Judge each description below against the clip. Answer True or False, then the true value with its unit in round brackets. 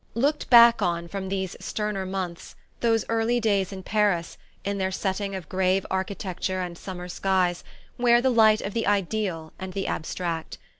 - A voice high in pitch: True (195 Hz)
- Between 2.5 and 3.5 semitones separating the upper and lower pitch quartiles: True (2.9 semitones)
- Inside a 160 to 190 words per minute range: True (165 wpm)